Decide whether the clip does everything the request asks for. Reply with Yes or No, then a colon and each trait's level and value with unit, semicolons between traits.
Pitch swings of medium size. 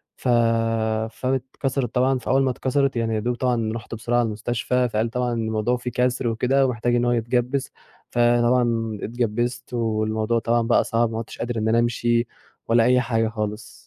No: narrow, 1.7 semitones